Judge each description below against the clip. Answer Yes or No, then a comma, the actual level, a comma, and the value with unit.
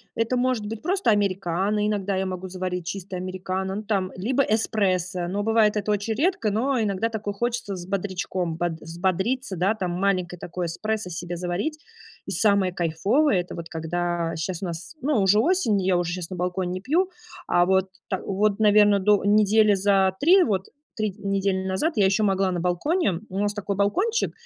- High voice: Yes, high, 195 Hz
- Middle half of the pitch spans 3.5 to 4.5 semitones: No, average, 2.9 semitones